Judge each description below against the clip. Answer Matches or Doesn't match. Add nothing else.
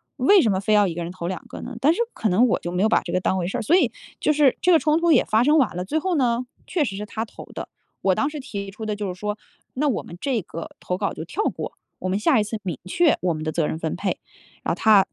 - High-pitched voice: Matches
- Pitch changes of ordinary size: Doesn't match